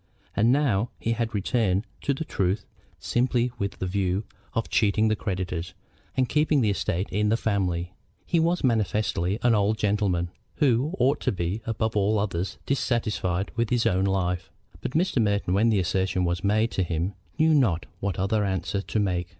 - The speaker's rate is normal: Yes, average, 180 wpm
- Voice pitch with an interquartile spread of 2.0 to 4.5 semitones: Yes, average, 3.8 semitones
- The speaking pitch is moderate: No, low, 105 Hz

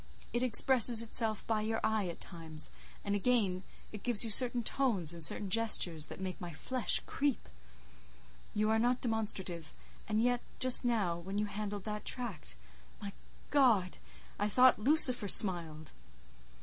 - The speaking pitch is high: Yes, high, 210 Hz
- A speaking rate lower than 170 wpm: Yes, average, 145 wpm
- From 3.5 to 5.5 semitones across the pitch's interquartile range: Yes, average, 4.8 semitones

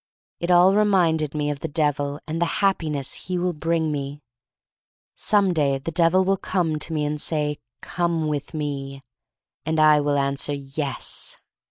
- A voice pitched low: No, medium, 155 Hz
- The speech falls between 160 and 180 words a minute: Yes, average, 165 wpm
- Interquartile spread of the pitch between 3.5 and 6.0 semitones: No, average, 3.0 semitones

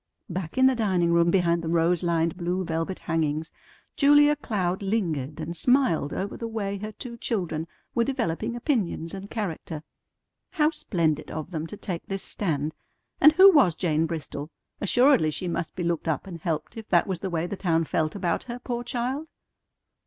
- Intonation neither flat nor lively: No, wide, 5.9 semitones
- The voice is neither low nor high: Yes, medium, 180 Hz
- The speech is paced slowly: No, average, 180 wpm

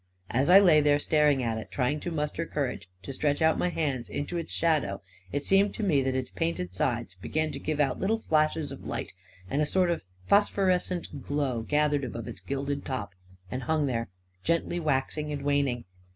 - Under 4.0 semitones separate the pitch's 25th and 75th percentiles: Yes, average, 3.6 semitones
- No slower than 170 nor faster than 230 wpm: Yes, average, 200 wpm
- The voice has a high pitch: No, medium, 145 Hz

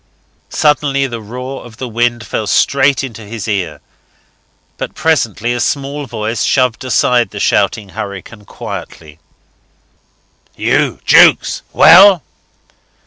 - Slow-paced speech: Yes, slow, 115 wpm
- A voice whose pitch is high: No, low, 120 Hz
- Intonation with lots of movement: No, average, 4.3 semitones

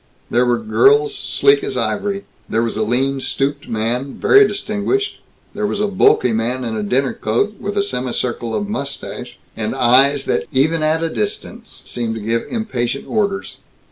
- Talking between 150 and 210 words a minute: Yes, average, 175 wpm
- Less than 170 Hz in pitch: Yes, medium, 140 Hz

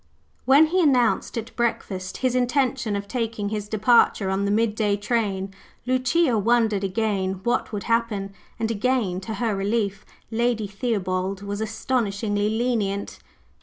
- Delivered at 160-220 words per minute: No, slow, 135 wpm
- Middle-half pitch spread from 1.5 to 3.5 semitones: Yes, average, 3.1 semitones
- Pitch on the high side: Yes, high, 220 Hz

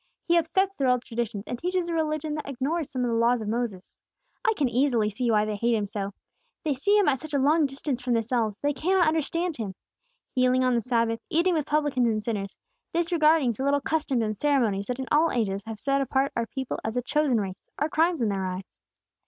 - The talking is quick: Yes, fast, 230 wpm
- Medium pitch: No, very high, 255 Hz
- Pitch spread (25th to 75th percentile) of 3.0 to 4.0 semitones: No, average, 5.2 semitones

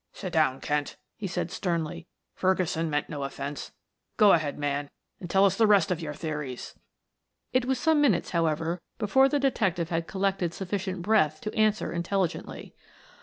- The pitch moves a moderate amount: Yes, average, 4.2 semitones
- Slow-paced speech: No, average, 165 wpm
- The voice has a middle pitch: Yes, medium, 175 Hz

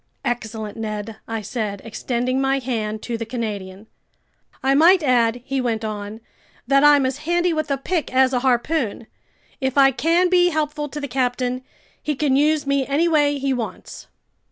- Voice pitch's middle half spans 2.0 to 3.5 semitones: No, average, 4.4 semitones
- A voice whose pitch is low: No, very high, 260 Hz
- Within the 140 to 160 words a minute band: No, average, 175 wpm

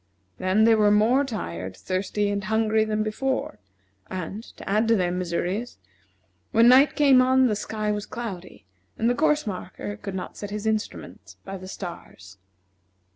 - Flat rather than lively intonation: No, average, 3.4 semitones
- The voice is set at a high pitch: Yes, high, 210 Hz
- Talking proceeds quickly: No, average, 165 wpm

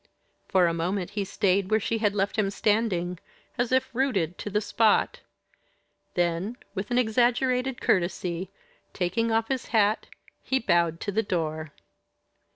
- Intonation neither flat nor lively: Yes, average, 4.3 semitones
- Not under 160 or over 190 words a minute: No, average, 150 wpm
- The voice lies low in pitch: No, high, 205 Hz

